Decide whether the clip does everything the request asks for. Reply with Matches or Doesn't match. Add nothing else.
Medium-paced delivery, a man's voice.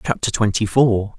Matches